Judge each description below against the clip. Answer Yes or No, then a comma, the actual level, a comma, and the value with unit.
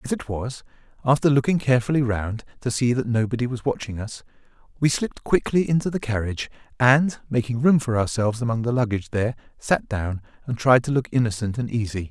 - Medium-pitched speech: No, low, 120 Hz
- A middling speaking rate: Yes, average, 190 wpm